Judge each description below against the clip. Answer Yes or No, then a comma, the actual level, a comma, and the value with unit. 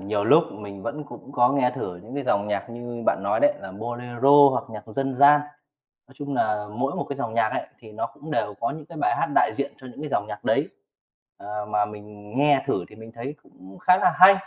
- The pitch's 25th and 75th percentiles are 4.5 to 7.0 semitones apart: Yes, average, 5.2 semitones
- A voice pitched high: No, low, 120 Hz